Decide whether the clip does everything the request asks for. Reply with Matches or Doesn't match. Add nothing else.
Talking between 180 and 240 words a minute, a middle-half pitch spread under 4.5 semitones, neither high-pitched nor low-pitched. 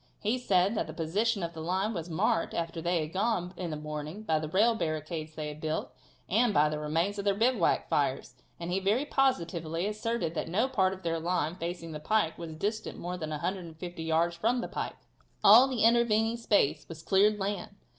Doesn't match